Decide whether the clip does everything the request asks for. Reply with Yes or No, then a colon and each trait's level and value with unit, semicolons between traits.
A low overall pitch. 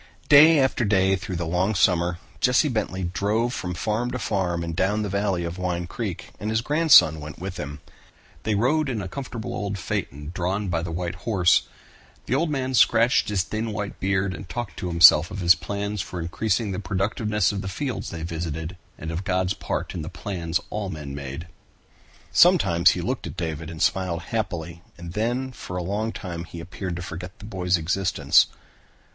Yes: very low, 95 Hz